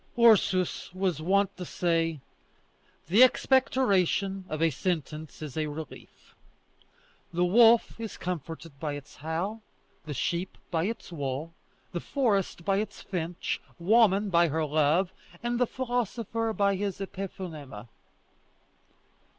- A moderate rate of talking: No, slow, 125 wpm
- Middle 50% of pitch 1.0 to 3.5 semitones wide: No, average, 4.4 semitones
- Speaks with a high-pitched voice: No, medium, 180 Hz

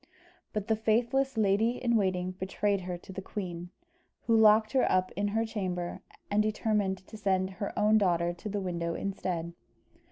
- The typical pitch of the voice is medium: No, high, 200 Hz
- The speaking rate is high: No, average, 170 wpm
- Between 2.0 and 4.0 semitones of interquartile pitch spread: Yes, average, 2.8 semitones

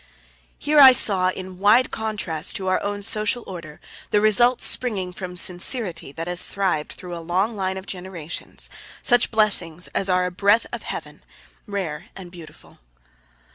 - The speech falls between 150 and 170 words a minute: Yes, average, 160 wpm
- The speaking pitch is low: No, high, 190 Hz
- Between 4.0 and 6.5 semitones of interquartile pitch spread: No, average, 3.1 semitones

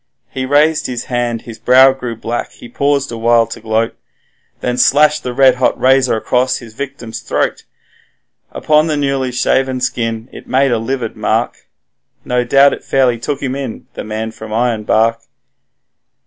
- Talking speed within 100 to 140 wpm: No, average, 165 wpm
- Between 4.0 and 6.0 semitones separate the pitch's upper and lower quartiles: No, average, 2.7 semitones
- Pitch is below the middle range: Yes, low, 125 Hz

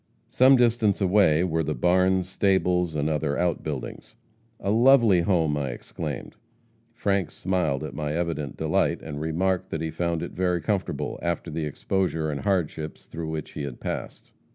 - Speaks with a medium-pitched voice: No, very low, 85 Hz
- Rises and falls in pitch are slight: No, average, 3.4 semitones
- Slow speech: No, average, 160 wpm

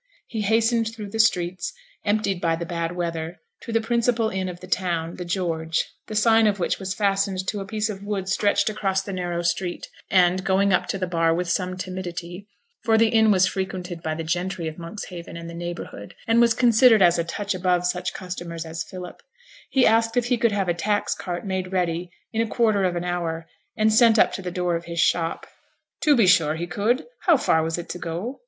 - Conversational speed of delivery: No, fast, 220 wpm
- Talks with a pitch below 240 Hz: Yes, medium, 185 Hz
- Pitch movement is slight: No, average, 3.7 semitones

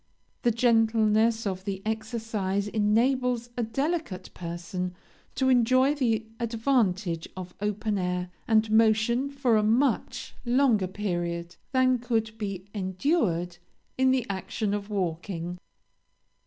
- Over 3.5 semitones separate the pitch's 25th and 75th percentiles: Yes, average, 4.3 semitones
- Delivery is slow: Yes, slow, 115 wpm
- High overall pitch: Yes, high, 220 Hz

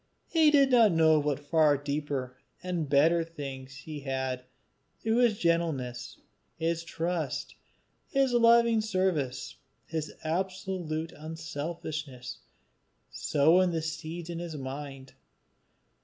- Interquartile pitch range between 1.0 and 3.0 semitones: No, average, 3.9 semitones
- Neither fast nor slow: No, slow, 110 wpm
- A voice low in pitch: No, medium, 160 Hz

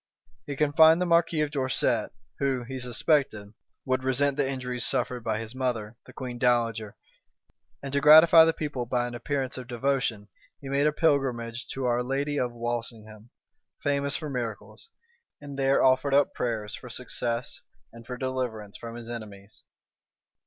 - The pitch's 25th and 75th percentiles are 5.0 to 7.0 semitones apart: No, average, 3.1 semitones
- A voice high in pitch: No, low, 125 Hz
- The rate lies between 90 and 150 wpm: No, average, 160 wpm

